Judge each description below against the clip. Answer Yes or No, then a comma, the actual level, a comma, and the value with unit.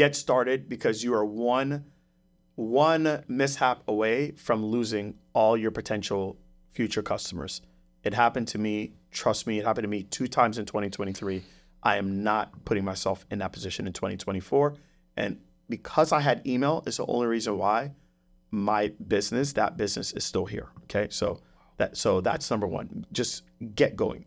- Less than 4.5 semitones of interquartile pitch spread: No, average, 4.8 semitones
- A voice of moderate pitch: No, low, 110 Hz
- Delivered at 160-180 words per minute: Yes, average, 165 wpm